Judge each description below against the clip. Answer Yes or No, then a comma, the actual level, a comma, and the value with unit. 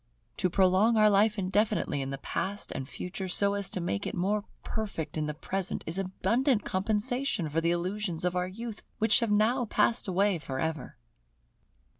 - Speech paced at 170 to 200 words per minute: Yes, average, 180 wpm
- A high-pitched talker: Yes, high, 195 Hz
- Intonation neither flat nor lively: Yes, average, 3.6 semitones